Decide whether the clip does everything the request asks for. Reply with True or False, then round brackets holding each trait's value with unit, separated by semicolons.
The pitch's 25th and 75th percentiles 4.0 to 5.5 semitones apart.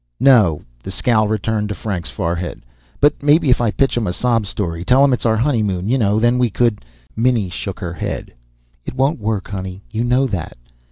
True (4.7 semitones)